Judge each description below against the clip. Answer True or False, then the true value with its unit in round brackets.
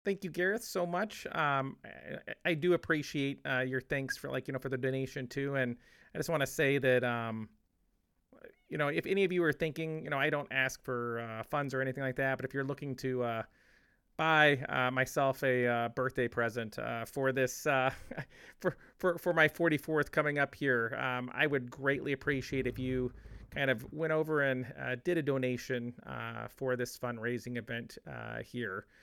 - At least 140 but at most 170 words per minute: False (200 wpm)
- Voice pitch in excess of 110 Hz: True (135 Hz)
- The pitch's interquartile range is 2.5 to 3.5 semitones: True (2.9 semitones)